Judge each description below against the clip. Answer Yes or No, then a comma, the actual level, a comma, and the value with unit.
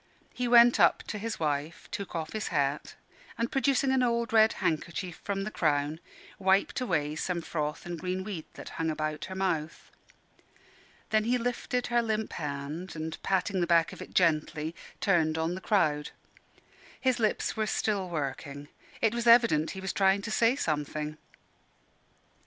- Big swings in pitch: Yes, wide, 6.0 semitones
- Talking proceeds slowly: No, average, 165 wpm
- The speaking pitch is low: No, medium, 185 Hz